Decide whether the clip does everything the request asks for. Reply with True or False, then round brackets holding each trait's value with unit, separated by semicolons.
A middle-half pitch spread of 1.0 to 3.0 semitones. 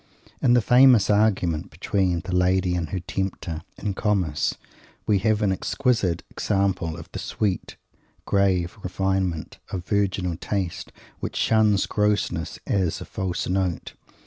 True (2.7 semitones)